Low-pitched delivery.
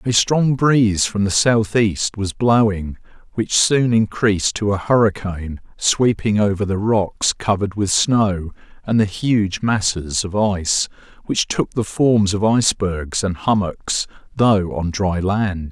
Yes: low, 105 Hz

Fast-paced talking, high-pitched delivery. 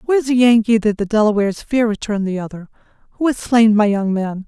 Yes: fast, 230 wpm; high, 220 Hz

